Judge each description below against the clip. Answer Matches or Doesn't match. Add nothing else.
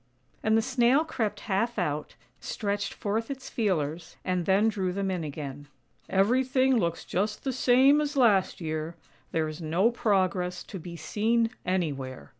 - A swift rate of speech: Doesn't match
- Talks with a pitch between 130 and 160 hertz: Doesn't match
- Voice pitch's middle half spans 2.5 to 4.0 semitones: Doesn't match